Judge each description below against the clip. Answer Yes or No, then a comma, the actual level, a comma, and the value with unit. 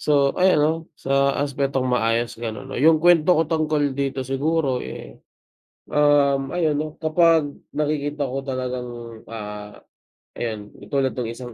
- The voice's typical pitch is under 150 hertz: Yes, medium, 140 Hz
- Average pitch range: Yes, average, 3.3 semitones